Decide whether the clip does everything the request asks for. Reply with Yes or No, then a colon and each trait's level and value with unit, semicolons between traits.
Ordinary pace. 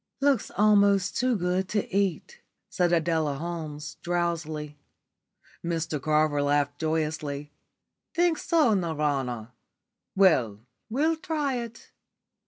No: slow, 100 wpm